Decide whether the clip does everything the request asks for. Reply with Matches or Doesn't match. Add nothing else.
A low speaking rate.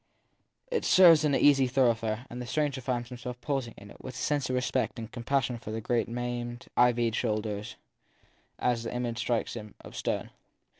Doesn't match